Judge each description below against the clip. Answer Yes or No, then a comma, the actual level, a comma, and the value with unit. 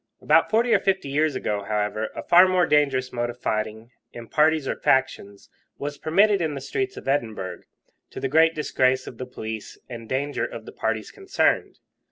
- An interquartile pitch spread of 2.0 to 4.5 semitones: No, wide, 5.6 semitones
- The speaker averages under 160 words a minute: No, average, 190 wpm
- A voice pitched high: No, low, 135 Hz